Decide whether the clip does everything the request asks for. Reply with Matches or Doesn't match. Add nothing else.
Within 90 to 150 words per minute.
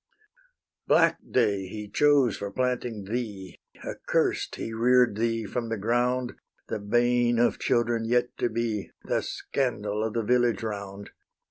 Matches